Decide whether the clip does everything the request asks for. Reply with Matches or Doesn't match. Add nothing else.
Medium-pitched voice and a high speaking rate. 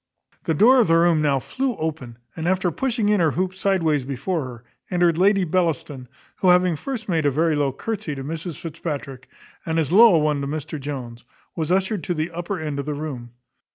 Matches